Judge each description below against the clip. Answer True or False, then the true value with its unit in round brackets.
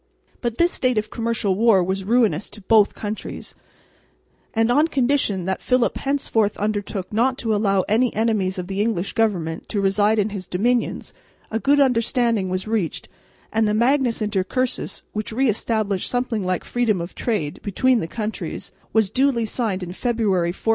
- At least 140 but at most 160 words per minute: False (170 wpm)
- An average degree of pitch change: True (3.5 semitones)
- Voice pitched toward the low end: False (220 Hz)